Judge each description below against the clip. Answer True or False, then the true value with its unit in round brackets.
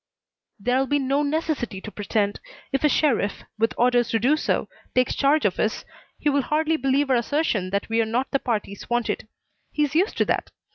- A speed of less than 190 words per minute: False (195 wpm)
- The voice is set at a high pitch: True (255 Hz)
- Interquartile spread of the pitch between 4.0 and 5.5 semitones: True (4.5 semitones)